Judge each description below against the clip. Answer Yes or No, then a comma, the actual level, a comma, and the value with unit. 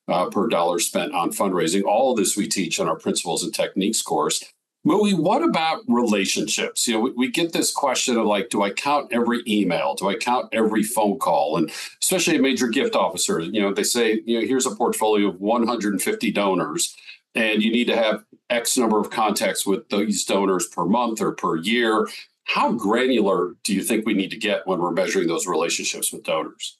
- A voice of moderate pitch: No, low, 115 Hz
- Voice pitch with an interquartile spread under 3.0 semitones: No, average, 3.6 semitones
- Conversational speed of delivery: No, fast, 210 wpm